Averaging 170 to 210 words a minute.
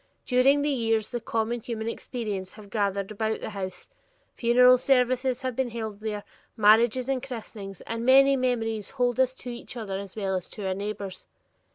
Yes: average, 180 wpm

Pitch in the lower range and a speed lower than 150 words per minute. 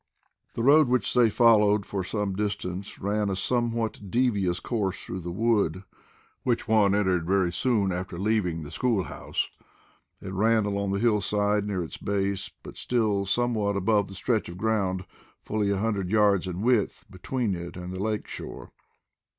No: low, 100 Hz; average, 165 wpm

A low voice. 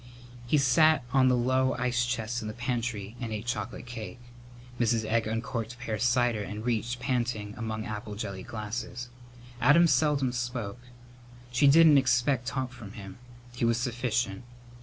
Yes: low, 120 Hz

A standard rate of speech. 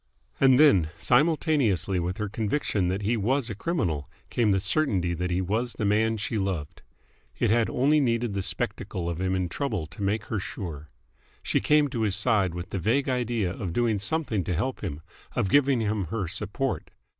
Yes: average, 190 wpm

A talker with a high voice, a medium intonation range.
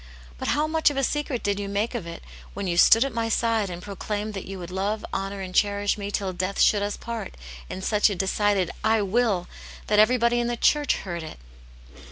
Yes: high, 205 Hz; average, 3.1 semitones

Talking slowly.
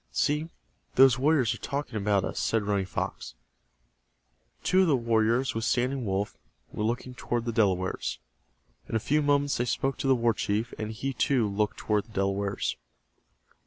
No: average, 170 wpm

